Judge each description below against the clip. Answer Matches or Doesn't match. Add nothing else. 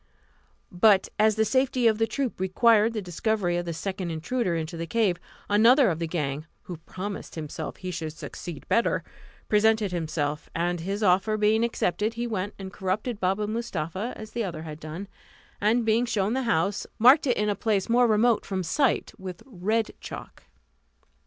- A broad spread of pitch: Doesn't match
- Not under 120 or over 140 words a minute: Doesn't match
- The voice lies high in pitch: Matches